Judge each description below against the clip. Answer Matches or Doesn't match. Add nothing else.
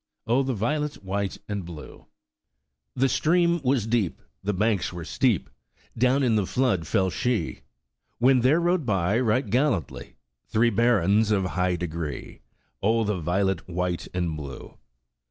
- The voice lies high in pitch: Doesn't match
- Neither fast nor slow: Matches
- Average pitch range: Doesn't match